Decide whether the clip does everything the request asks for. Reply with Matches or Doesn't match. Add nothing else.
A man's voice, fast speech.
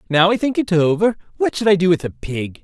Matches